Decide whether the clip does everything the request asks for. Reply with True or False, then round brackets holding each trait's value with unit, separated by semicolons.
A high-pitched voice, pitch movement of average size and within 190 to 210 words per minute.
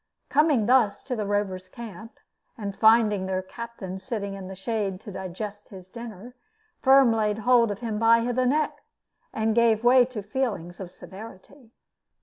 False (220 Hz; 3.3 semitones; 160 wpm)